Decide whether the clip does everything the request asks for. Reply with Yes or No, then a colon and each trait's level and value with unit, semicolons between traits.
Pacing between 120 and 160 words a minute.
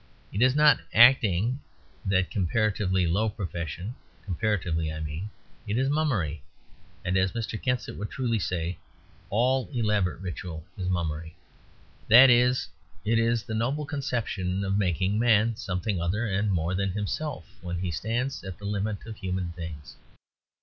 Yes: average, 150 wpm